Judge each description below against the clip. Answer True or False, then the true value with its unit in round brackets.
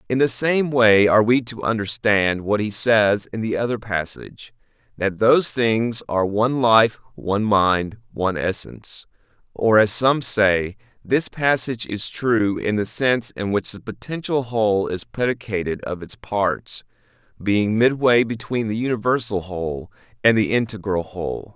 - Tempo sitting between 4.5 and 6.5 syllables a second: True (4.6 syllables/s)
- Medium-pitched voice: False (110 Hz)